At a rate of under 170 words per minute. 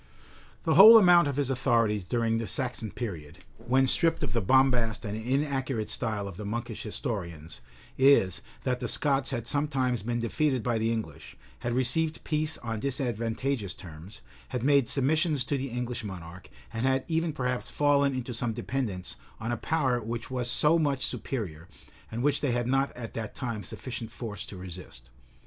No: average, 175 wpm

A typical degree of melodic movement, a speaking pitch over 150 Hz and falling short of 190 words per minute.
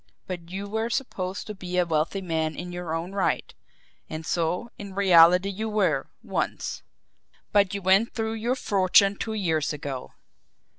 Yes: average, 3.2 semitones; medium, 185 Hz; average, 160 wpm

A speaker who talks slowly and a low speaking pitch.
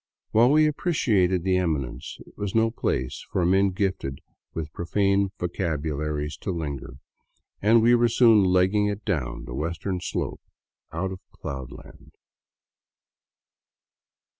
Yes: slow, 125 wpm; very low, 95 Hz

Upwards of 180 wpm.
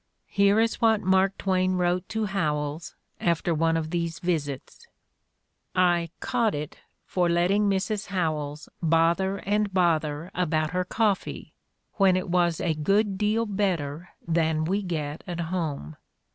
No: average, 140 wpm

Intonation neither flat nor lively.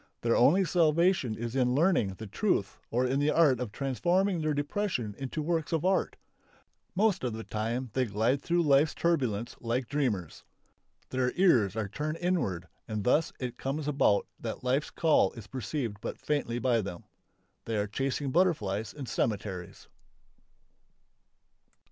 No: wide, 5.7 semitones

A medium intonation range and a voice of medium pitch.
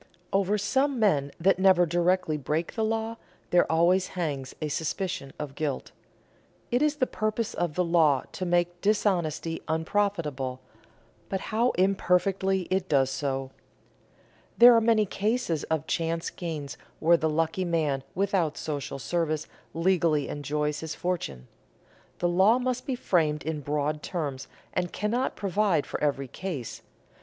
Yes: average, 4.6 semitones; medium, 170 Hz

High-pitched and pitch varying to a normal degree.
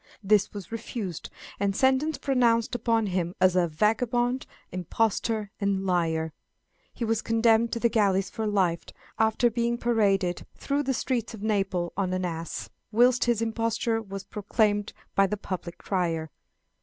Yes: high, 210 Hz; average, 3.7 semitones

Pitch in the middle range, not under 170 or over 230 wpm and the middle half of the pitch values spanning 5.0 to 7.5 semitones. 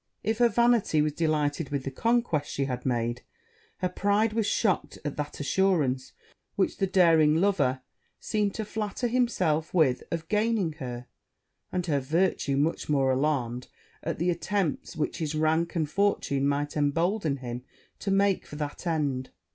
No: medium, 160 Hz; average, 160 wpm; wide, 5.6 semitones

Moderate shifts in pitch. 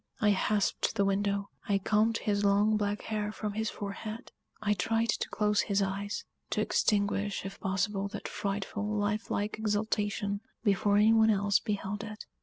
No: narrow, 1.1 semitones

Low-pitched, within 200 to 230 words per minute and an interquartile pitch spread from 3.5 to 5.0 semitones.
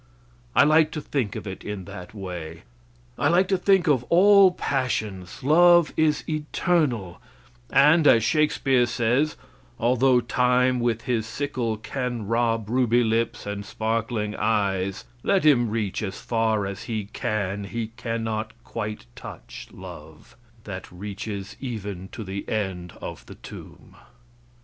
No: low, 115 Hz; average, 140 wpm; average, 4.7 semitones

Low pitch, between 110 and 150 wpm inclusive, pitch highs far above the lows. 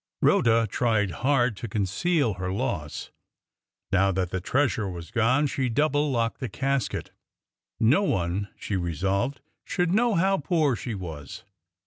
Yes: low, 115 Hz; average, 140 wpm; wide, 6.8 semitones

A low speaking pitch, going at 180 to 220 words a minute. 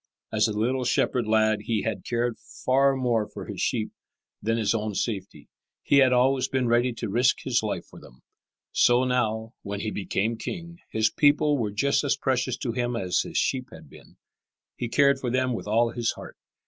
Yes: low, 120 Hz; average, 200 wpm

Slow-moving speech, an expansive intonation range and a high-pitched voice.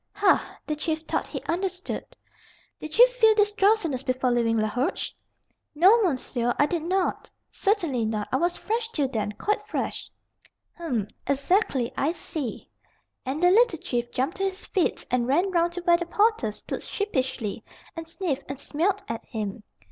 No: average, 165 wpm; wide, 7.3 semitones; very high, 325 Hz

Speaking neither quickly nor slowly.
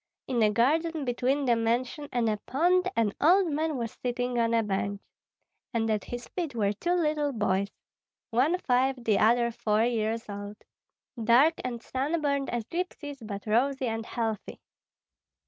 Yes: average, 160 wpm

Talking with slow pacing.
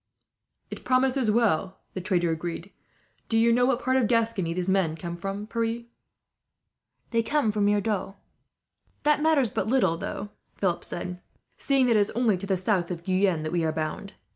No: average, 175 wpm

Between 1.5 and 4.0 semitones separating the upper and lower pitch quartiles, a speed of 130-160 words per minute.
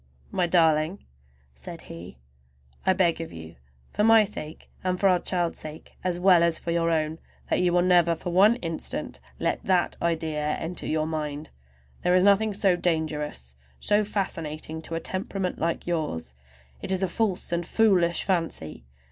No: average, 2.9 semitones; average, 170 wpm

